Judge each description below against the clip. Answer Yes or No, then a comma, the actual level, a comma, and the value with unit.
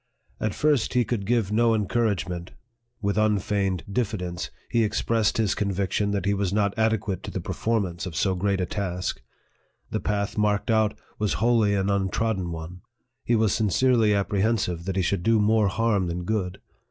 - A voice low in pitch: Yes, low, 100 Hz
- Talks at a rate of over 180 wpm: No, average, 175 wpm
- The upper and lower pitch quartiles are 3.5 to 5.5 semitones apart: No, narrow, 2.6 semitones